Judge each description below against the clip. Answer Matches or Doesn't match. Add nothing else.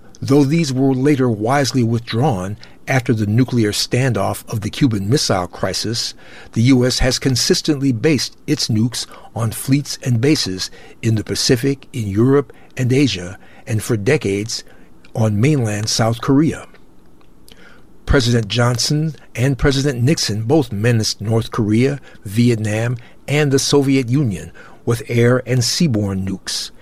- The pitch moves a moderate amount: Matches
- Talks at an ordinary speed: Doesn't match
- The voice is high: Doesn't match